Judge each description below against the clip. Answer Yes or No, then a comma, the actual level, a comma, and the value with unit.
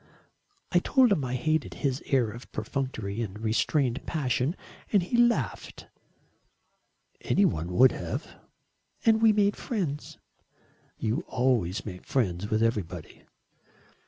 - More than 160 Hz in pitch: No, low, 130 Hz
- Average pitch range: No, wide, 8.0 semitones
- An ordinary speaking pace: No, slow, 125 wpm